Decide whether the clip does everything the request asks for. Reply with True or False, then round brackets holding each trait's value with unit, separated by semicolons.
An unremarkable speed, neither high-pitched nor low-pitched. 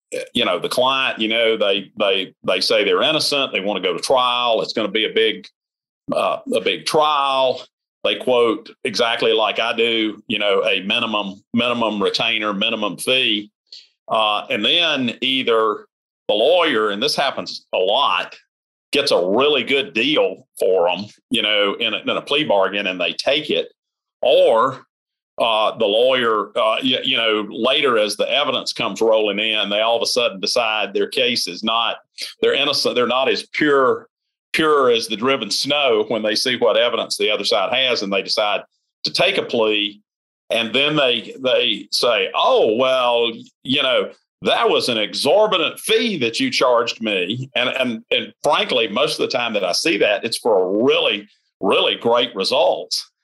True (180 wpm; 155 Hz)